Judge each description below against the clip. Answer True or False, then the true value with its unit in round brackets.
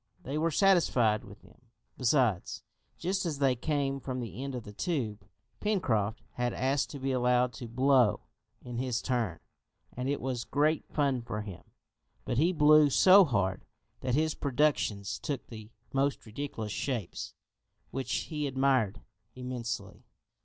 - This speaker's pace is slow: False (150 wpm)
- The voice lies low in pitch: True (130 Hz)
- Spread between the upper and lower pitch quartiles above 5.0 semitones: False (4.1 semitones)